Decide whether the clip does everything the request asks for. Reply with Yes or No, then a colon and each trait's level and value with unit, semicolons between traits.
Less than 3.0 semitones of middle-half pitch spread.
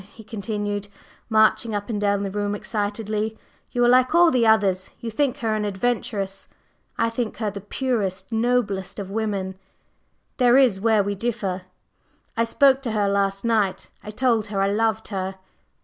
Yes: narrow, 2.6 semitones